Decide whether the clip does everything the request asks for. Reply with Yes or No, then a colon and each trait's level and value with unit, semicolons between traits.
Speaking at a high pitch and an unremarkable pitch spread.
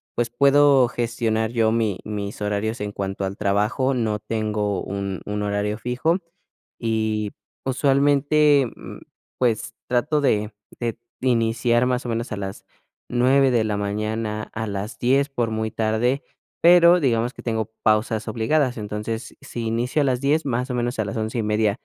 No: low, 115 Hz; average, 3.0 semitones